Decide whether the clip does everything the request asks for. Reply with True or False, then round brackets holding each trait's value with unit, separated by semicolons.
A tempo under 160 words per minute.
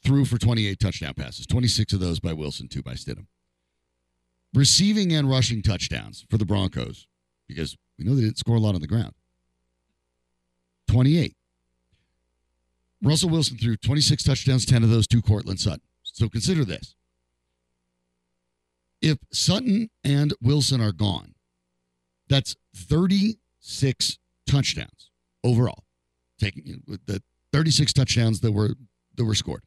True (135 wpm)